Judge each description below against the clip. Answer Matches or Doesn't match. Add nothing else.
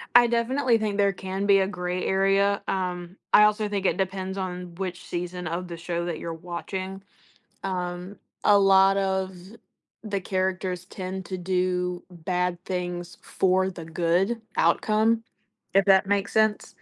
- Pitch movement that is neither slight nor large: Doesn't match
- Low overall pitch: Doesn't match